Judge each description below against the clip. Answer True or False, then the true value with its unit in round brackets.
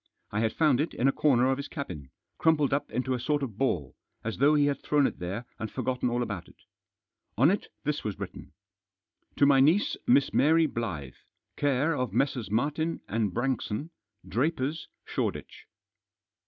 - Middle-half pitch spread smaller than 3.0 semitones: False (4.3 semitones)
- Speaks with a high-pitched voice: False (135 Hz)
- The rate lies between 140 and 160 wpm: False (180 wpm)